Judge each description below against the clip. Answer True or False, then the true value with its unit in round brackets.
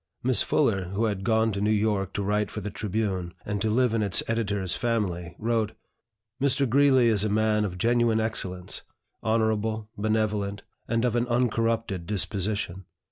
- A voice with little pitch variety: True (2.3 semitones)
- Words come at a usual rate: True (165 wpm)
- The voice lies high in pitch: False (110 Hz)